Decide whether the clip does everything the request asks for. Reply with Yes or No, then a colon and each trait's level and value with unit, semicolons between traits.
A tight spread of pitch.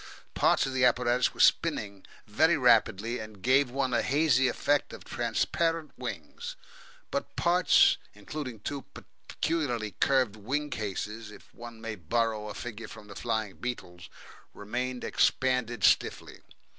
No: average, 3.9 semitones